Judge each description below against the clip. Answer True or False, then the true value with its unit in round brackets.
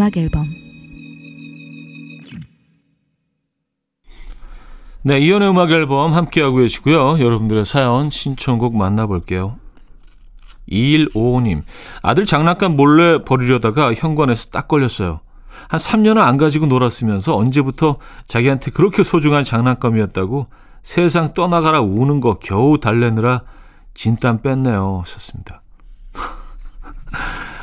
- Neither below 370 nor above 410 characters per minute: False (240 characters per minute)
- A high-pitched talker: False (130 Hz)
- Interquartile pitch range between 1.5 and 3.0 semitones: False (5.5 semitones)